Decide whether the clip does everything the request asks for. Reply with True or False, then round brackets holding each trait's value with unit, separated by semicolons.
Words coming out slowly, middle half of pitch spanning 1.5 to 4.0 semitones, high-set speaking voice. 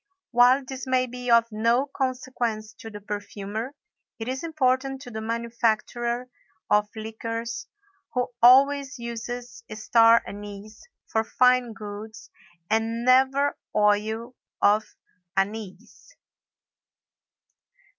True (105 wpm; 2.7 semitones; 235 Hz)